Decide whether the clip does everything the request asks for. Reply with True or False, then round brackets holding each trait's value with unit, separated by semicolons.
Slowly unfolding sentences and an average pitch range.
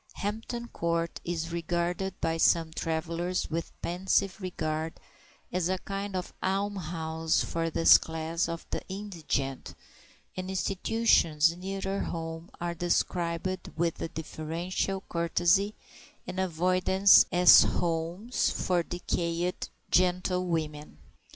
False (105 wpm; 2.3 semitones)